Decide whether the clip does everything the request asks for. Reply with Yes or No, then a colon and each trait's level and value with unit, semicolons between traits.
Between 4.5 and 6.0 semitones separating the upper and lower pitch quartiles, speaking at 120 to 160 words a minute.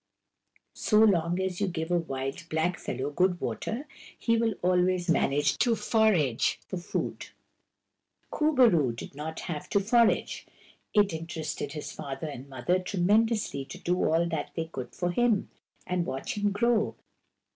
Yes: average, 5.1 semitones; average, 155 wpm